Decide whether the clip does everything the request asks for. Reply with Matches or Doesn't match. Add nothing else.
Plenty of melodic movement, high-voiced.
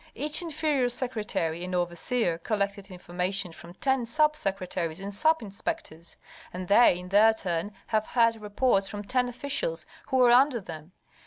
Matches